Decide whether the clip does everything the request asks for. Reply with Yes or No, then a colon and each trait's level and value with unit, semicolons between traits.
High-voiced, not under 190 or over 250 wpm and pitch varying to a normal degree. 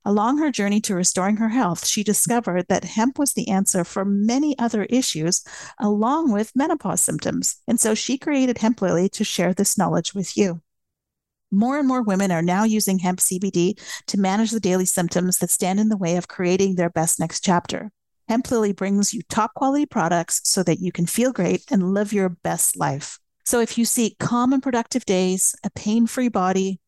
Yes: high, 205 Hz; average, 200 wpm; average, 4.1 semitones